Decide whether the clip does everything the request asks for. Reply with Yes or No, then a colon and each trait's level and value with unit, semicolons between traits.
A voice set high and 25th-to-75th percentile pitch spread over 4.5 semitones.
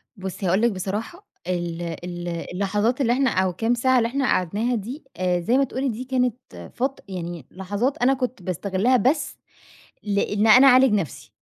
Yes: high, 215 Hz; wide, 5.5 semitones